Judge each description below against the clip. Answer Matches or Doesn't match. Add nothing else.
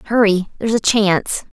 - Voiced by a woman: Matches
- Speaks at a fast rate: Doesn't match